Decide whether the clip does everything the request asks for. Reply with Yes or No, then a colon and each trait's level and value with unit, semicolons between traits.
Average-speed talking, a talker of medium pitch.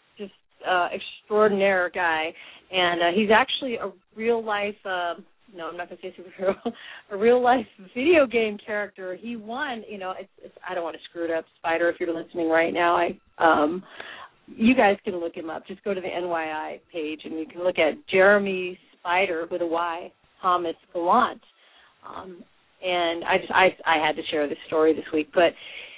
Yes: average, 195 wpm; medium, 180 Hz